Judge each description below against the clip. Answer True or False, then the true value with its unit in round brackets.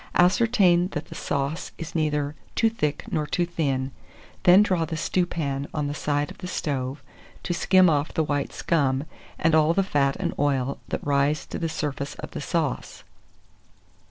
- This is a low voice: False (150 Hz)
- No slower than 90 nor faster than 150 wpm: False (175 wpm)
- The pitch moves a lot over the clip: False (3.4 semitones)